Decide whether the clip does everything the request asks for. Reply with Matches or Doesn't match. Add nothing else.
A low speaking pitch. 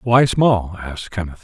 Matches